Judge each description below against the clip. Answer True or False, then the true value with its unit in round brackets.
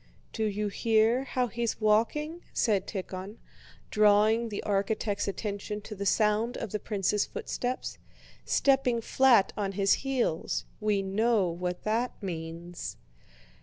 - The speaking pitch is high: True (210 Hz)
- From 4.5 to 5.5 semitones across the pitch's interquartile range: False (2.9 semitones)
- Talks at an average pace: False (125 wpm)